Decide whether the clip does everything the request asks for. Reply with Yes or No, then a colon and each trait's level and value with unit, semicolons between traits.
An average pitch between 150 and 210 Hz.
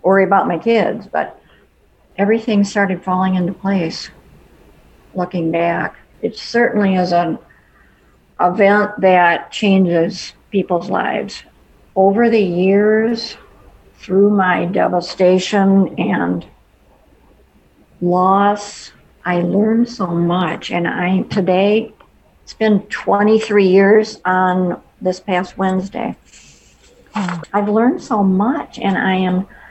Yes: high, 190 Hz